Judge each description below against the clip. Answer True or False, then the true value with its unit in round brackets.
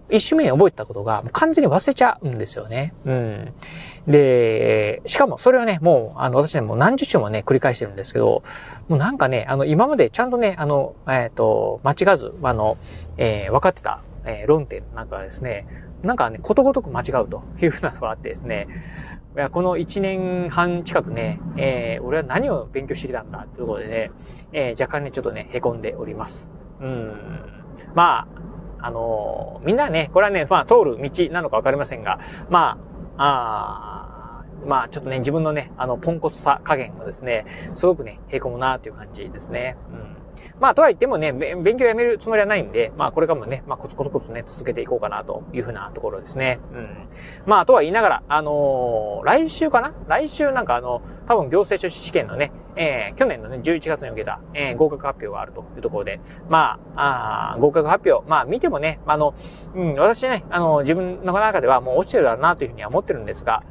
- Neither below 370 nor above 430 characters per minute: True (400 characters per minute)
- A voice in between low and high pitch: True (160 Hz)